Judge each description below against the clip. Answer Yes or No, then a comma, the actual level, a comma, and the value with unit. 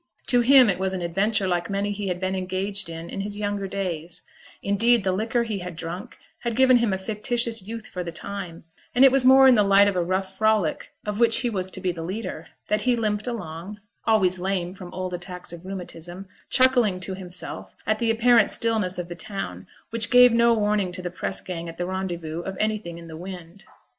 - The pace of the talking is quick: Yes, fast, 225 wpm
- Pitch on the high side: Yes, high, 195 Hz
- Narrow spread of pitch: No, average, 3.5 semitones